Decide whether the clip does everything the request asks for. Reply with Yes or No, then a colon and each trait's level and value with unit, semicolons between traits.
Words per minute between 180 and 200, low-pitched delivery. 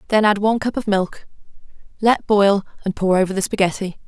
No: average, 190 wpm; high, 200 Hz